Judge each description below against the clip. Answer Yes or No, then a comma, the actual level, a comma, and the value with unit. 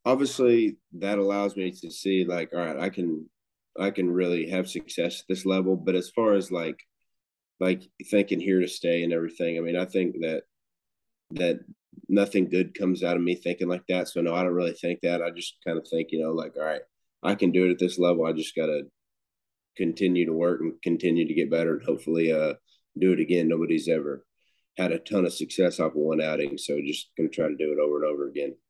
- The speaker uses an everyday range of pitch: No, narrow, 2.1 semitones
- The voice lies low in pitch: Yes, very low, 90 Hz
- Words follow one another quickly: Yes, fast, 230 wpm